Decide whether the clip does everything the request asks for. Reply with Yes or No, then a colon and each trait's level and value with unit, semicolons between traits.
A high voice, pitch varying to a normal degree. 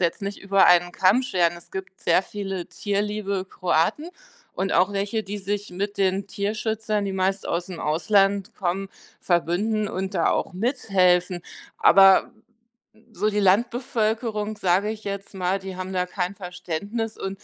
No: high, 195 Hz; narrow, 2.2 semitones